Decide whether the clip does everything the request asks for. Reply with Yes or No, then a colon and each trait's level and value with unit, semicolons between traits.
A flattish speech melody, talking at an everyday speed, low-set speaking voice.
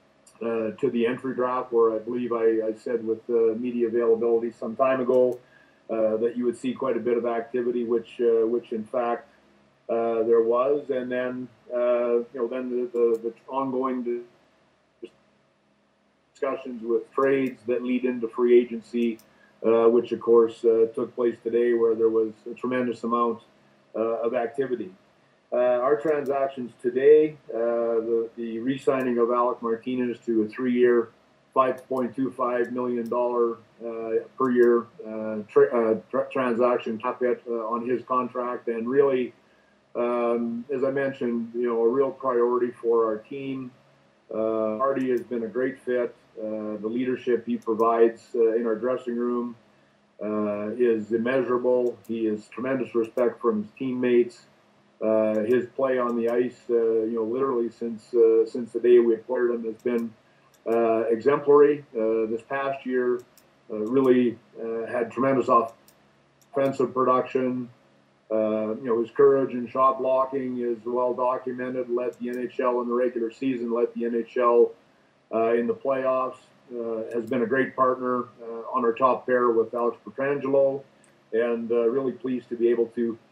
Yes: narrow, 1.7 semitones; average, 160 wpm; low, 120 Hz